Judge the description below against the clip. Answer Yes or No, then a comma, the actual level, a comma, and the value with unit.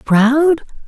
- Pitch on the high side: Yes, very high, 275 Hz